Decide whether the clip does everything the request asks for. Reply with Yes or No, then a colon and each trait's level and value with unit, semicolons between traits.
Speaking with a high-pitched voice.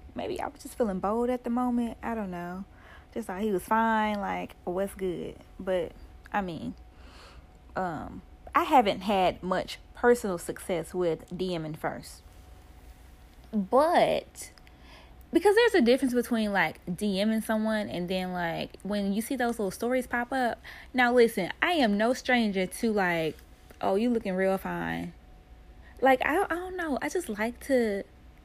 Yes: high, 210 Hz